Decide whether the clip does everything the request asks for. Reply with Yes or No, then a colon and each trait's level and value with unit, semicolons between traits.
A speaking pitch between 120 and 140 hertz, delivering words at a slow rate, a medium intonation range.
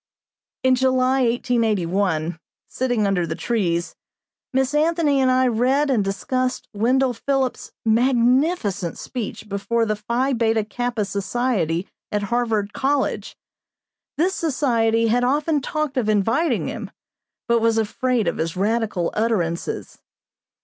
No: high, 235 Hz; slow, 120 wpm; average, 4.1 semitones